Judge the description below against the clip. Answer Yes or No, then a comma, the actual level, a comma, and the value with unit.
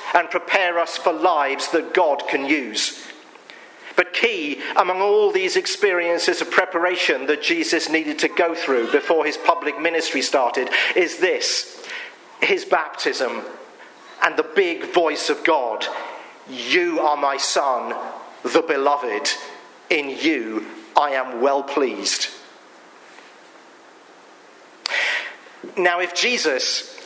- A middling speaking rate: No, slow, 120 wpm